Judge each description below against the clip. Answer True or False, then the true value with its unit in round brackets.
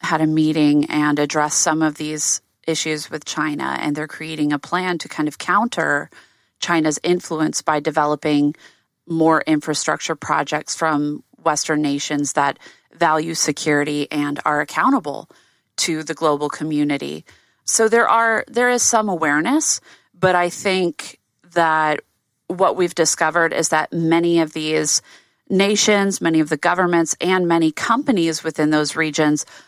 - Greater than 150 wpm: False (140 wpm)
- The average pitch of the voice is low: False (155 Hz)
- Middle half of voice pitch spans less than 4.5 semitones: True (2.4 semitones)